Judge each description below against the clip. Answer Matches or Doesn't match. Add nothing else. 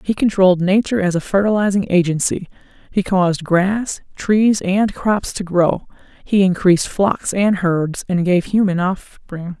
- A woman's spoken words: Matches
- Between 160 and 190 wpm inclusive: Doesn't match